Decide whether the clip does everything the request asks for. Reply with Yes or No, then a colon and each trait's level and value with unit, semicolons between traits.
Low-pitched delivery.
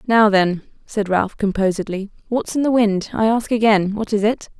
No: high, 210 Hz